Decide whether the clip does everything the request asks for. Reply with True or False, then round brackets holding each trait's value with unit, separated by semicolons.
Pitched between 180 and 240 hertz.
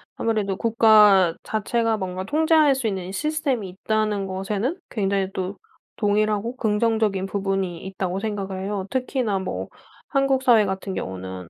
True (205 Hz)